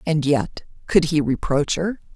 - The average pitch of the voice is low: No, medium, 155 Hz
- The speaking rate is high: No, average, 165 wpm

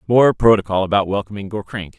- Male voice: Yes, male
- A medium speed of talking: Yes, average, 150 wpm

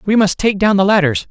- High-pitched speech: Yes, high, 195 Hz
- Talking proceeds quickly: Yes, fast, 275 wpm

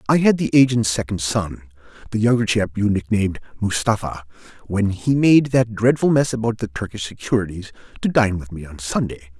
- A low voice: Yes, low, 105 Hz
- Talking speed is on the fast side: No, average, 180 wpm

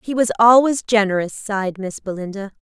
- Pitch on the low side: No, high, 210 Hz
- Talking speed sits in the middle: Yes, average, 160 wpm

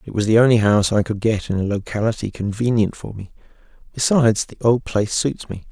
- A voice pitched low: Yes, low, 110 Hz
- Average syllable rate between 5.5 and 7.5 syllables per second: Yes, 6.0 syllables/s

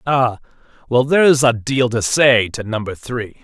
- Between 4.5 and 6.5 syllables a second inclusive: No, 4.3 syllables/s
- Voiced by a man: Yes, male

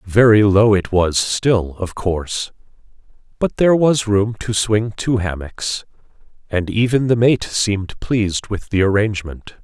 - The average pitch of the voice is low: Yes, low, 105 Hz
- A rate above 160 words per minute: No, average, 150 wpm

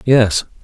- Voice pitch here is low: Yes, low, 105 Hz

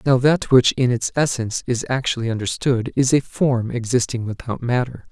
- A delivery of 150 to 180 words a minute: Yes, average, 175 wpm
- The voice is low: Yes, low, 125 Hz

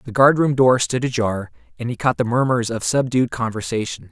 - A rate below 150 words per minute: No, average, 190 wpm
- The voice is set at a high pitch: No, low, 120 Hz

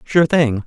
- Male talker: Yes, male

